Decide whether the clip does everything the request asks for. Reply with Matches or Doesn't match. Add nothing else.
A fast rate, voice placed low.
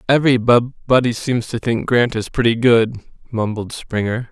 Doesn't match